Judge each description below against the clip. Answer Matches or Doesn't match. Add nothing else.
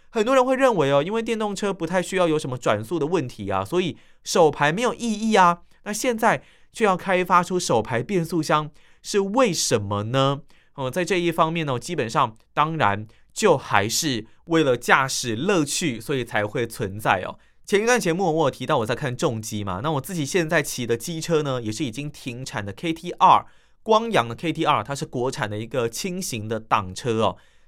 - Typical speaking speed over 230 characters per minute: Matches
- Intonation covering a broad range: Matches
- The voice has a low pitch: Doesn't match